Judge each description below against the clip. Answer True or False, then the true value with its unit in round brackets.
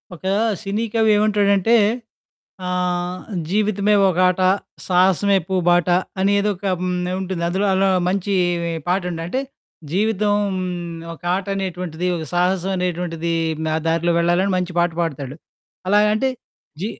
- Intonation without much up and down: True (2.3 semitones)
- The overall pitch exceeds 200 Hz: False (185 Hz)